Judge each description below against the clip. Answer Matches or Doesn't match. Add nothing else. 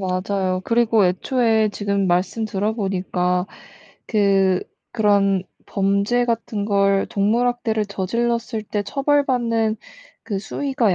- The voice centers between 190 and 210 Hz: Matches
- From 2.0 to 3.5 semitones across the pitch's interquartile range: Matches